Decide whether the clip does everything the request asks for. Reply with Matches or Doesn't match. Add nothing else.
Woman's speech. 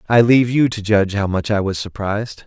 Doesn't match